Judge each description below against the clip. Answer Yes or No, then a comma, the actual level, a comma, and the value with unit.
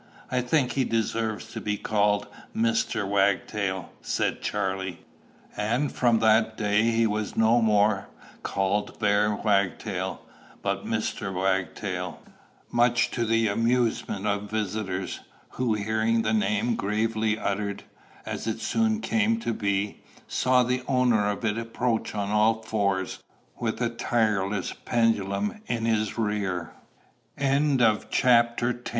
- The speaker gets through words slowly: Yes, slow, 120 wpm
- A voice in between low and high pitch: No, low, 110 Hz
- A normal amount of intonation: No, narrow, 2.3 semitones